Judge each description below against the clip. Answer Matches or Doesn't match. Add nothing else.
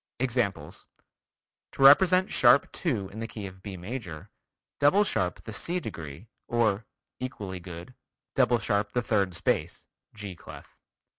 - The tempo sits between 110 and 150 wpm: Matches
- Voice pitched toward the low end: Matches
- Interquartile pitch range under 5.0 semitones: Doesn't match